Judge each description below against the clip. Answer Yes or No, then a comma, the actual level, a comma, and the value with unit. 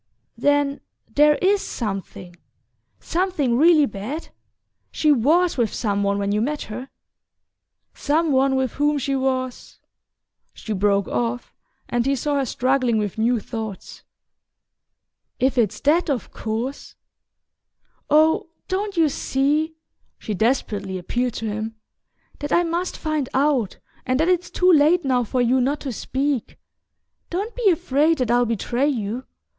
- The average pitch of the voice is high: Yes, very high, 265 Hz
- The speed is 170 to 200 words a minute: No, average, 140 wpm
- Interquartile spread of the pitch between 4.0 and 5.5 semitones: Yes, average, 4.7 semitones